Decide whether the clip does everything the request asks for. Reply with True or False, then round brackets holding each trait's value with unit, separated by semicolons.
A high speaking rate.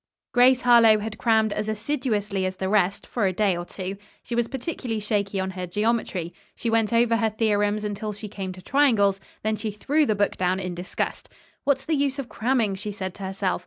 True (210 wpm)